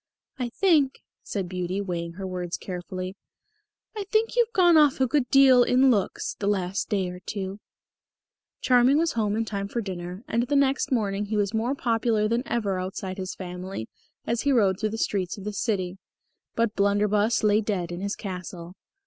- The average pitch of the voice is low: No, high, 205 Hz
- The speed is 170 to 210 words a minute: Yes, average, 185 wpm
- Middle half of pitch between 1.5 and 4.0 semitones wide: No, average, 4.4 semitones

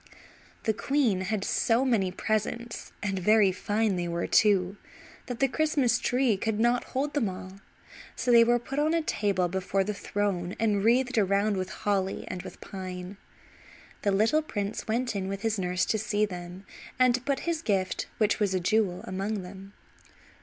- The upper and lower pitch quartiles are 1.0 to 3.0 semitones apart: No, average, 3.8 semitones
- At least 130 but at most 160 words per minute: No, average, 180 wpm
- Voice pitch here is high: Yes, high, 205 Hz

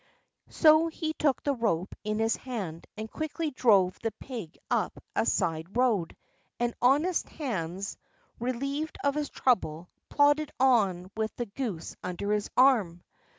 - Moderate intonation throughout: No, wide, 6.5 semitones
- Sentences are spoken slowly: No, average, 145 wpm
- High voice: Yes, high, 235 Hz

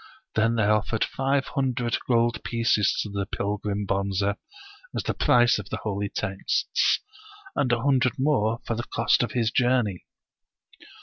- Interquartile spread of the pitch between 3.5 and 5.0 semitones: No, average, 3.1 semitones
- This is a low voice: Yes, low, 115 Hz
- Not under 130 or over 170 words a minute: Yes, average, 150 wpm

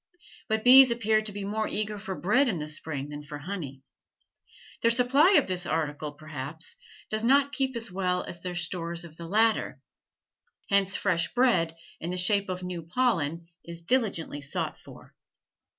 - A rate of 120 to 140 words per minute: No, average, 170 wpm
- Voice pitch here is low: No, medium, 185 Hz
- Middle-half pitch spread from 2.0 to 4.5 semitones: No, average, 5.1 semitones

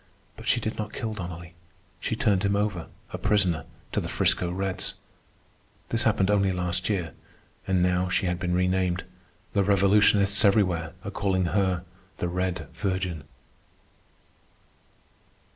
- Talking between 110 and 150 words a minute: Yes, average, 140 wpm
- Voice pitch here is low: Yes, very low, 95 Hz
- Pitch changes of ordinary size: No, narrow, 2.1 semitones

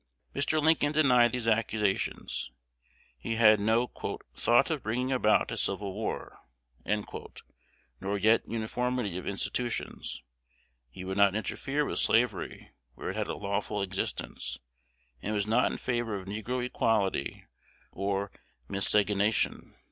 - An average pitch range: Yes, average, 3.6 semitones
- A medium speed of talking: No, slow, 125 wpm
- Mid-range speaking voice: No, low, 110 Hz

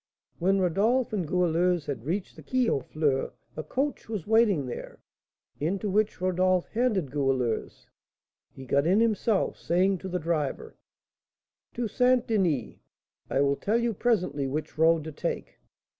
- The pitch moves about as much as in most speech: No, wide, 6.3 semitones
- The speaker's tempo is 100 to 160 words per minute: Yes, average, 150 wpm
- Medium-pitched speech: Yes, medium, 180 Hz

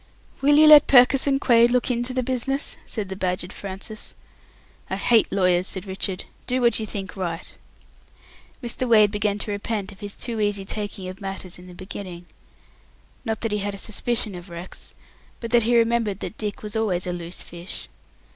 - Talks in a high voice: Yes, high, 210 Hz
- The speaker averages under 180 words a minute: No, average, 195 wpm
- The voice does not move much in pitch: No, average, 3.8 semitones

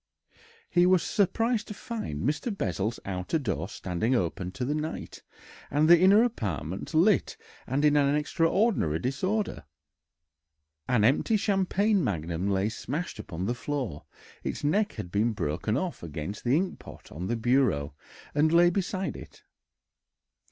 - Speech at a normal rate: Yes, average, 145 wpm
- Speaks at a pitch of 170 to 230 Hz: No, medium, 140 Hz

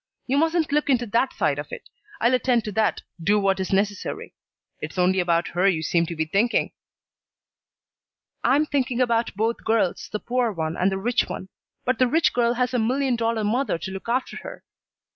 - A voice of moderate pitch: No, high, 230 Hz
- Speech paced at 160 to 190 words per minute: No, average, 200 wpm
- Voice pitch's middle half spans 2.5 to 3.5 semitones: No, average, 4.8 semitones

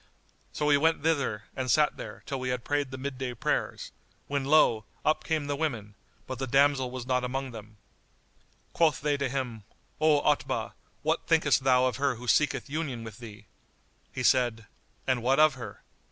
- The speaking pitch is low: Yes, low, 130 Hz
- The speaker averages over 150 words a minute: Yes, average, 180 wpm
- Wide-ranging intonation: No, average, 2.8 semitones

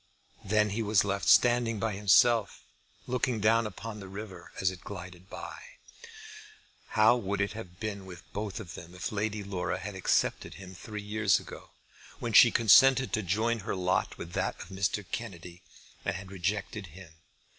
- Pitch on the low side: Yes, low, 100 Hz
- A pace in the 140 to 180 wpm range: Yes, average, 170 wpm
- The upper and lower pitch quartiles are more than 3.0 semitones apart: No, average, 2.7 semitones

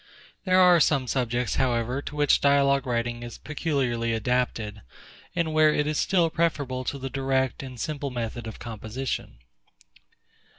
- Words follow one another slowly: No, average, 145 wpm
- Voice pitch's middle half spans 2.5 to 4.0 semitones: Yes, average, 3.6 semitones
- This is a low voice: Yes, low, 130 Hz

